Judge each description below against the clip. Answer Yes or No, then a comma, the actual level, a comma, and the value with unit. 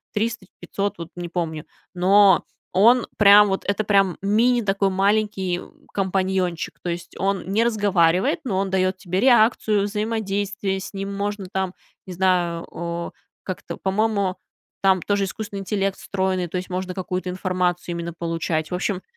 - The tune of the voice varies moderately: No, narrow, 2.1 semitones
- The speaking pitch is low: No, high, 190 Hz